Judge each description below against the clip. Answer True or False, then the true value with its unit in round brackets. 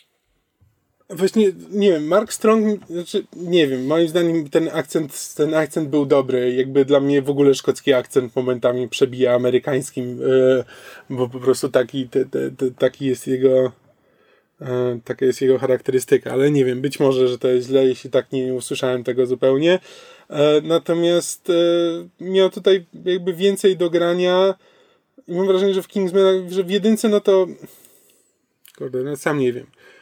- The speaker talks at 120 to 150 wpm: False (160 wpm)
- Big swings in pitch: True (6.4 semitones)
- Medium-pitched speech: True (150 Hz)